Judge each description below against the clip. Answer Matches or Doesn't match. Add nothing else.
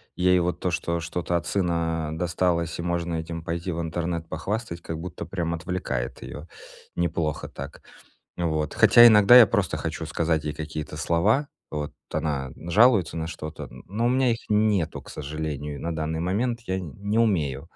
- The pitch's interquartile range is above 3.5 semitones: Doesn't match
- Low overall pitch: Matches